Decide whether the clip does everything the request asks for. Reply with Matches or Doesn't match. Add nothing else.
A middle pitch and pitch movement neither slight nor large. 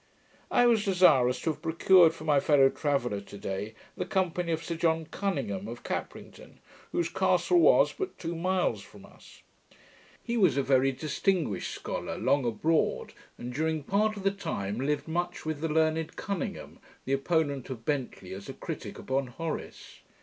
Matches